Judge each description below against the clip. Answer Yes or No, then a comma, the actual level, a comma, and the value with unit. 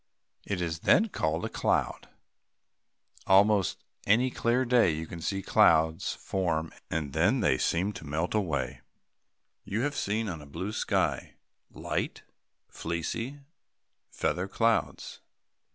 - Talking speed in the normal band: No, slow, 120 wpm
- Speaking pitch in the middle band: No, very low, 95 Hz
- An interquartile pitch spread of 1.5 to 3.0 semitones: No, average, 5.3 semitones